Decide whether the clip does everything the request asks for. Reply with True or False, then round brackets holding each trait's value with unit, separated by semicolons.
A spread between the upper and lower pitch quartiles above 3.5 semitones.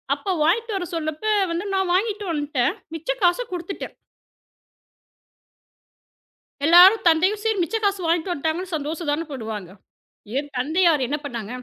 True (4.3 semitones)